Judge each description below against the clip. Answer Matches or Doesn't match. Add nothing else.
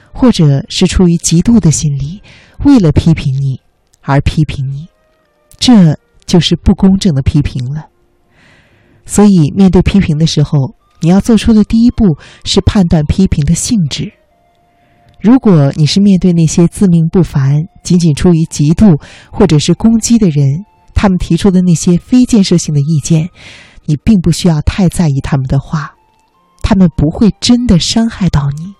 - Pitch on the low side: Doesn't match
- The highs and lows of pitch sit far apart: Doesn't match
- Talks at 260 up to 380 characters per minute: Doesn't match